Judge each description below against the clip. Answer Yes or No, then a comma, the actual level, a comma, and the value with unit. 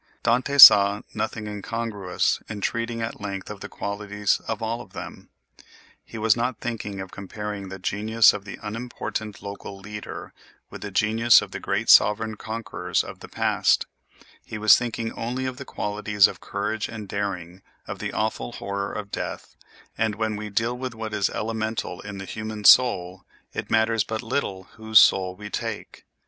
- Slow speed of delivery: No, average, 175 wpm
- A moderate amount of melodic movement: No, narrow, 2.0 semitones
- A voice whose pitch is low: Yes, low, 105 Hz